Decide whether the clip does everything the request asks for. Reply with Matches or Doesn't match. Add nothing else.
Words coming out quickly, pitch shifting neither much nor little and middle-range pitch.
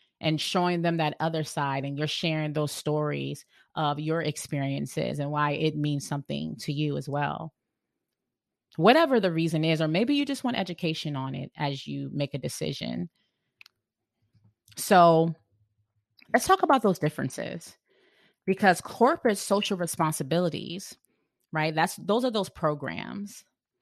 Doesn't match